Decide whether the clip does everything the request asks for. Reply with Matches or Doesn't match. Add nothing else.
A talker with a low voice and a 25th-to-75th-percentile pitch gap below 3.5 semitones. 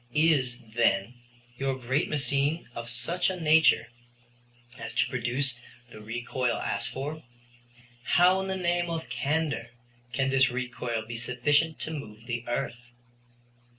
Doesn't match